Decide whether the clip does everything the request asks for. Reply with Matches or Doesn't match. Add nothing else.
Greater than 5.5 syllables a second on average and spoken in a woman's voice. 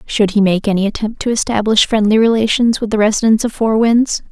Matches